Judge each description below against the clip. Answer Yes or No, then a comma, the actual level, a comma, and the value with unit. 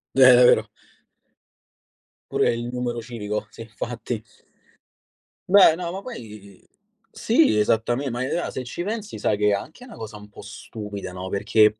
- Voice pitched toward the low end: Yes, low, 115 Hz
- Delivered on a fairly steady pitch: No, average, 4.9 semitones